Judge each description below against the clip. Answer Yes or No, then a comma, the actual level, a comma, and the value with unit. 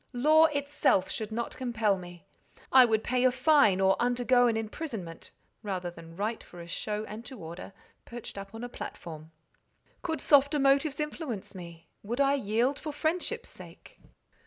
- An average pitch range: No, wide, 6.3 semitones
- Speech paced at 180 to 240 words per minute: No, average, 165 wpm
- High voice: Yes, high, 235 Hz